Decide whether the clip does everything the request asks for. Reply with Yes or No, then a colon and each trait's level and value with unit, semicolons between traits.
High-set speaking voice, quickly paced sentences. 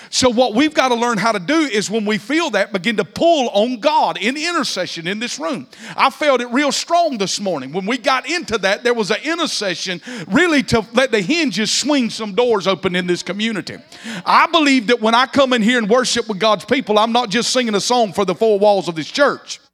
Yes: high, 235 Hz; fast, 235 wpm